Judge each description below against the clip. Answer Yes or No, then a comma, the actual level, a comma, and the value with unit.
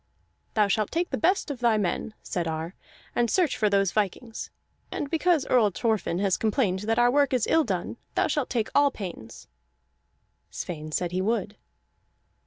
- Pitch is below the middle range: No, high, 220 Hz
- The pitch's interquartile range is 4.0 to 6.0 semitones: Yes, wide, 5.4 semitones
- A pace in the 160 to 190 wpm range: Yes, average, 175 wpm